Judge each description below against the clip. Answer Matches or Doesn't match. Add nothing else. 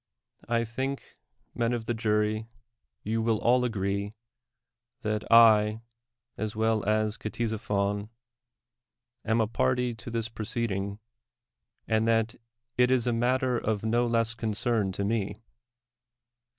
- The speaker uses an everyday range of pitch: Doesn't match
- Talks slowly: Matches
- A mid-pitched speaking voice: Doesn't match